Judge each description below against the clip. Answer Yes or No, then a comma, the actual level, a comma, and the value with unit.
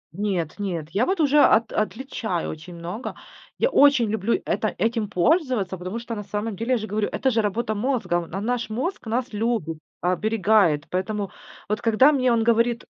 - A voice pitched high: Yes, high, 220 Hz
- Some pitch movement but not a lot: Yes, average, 3.9 semitones